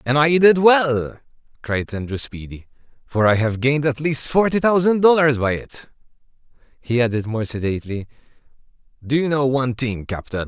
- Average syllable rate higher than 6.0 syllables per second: No, 5.1 syllables/s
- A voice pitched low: Yes, low, 130 Hz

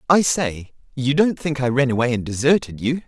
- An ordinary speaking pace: No, fast, 215 wpm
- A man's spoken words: Yes, male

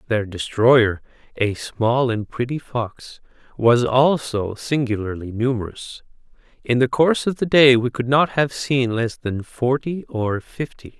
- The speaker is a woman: No, male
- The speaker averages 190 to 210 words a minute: No, average, 145 wpm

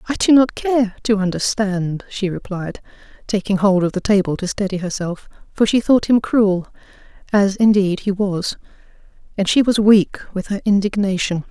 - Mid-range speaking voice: No, high, 200 Hz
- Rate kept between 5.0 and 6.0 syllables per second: No, 4.8 syllables/s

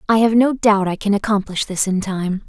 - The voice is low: No, high, 205 Hz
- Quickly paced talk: Yes, fast, 240 wpm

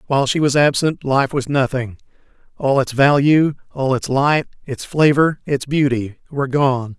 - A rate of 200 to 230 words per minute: No, average, 165 wpm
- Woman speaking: No, male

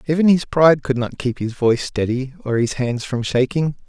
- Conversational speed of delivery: No, fast, 215 wpm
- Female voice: No, male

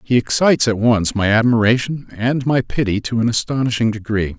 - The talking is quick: No, average, 180 wpm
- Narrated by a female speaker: No, male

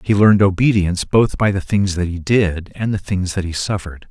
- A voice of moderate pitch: No, very low, 95 Hz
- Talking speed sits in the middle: No, fast, 235 wpm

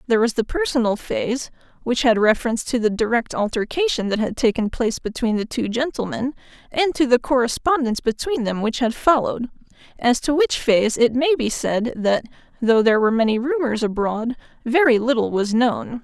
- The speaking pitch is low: No, high, 240 Hz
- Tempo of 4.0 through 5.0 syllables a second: No, 5.6 syllables/s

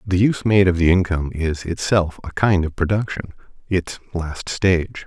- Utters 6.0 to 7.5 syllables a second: No, 5.0 syllables/s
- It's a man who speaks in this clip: Yes, male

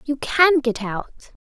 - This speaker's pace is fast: No, average, 165 wpm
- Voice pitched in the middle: No, very high, 265 Hz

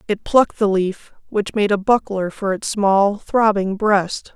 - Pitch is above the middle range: Yes, high, 205 Hz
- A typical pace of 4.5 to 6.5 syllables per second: No, 4.0 syllables/s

